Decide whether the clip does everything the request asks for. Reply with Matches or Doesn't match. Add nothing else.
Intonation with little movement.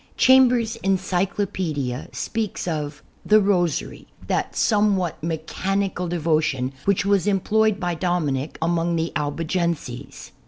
Doesn't match